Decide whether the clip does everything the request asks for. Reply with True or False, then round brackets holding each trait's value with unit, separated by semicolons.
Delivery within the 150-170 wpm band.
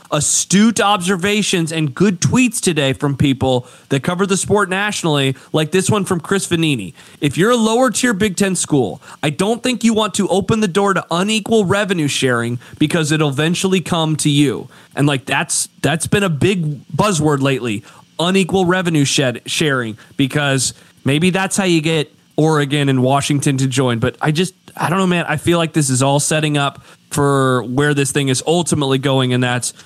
False (185 wpm)